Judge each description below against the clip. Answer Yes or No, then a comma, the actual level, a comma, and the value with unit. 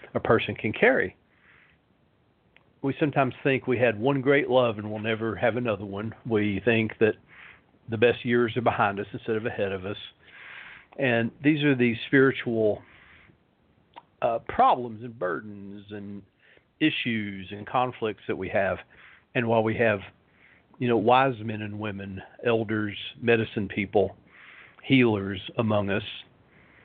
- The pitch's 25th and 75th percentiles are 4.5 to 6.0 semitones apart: No, average, 3.0 semitones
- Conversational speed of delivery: Yes, average, 145 wpm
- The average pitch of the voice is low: Yes, low, 115 Hz